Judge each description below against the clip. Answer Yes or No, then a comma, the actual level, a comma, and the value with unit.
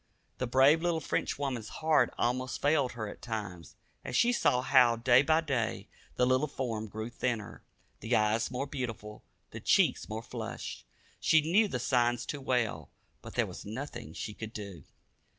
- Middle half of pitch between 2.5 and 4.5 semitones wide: Yes, average, 3.7 semitones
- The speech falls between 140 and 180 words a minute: Yes, average, 170 wpm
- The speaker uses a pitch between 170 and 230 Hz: No, low, 125 Hz